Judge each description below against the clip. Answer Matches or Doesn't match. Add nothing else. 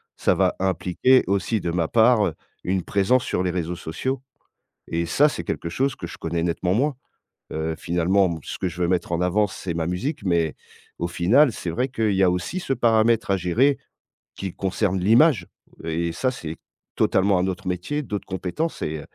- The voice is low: Matches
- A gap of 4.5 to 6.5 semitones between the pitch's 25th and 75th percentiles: Matches